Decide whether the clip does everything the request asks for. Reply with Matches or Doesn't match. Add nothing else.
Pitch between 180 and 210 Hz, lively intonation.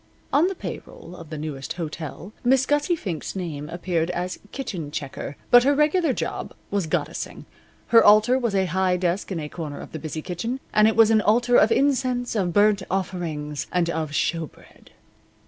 Matches